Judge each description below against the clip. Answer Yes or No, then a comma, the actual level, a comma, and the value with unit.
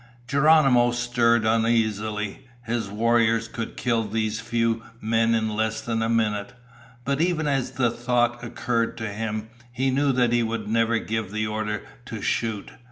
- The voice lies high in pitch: No, low, 115 Hz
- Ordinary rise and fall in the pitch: No, narrow, 1.6 semitones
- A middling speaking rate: Yes, average, 160 wpm